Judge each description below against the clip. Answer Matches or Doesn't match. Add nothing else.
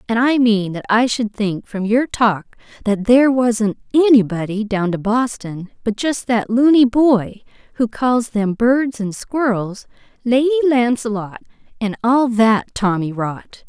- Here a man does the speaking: Doesn't match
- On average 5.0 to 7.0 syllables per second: Doesn't match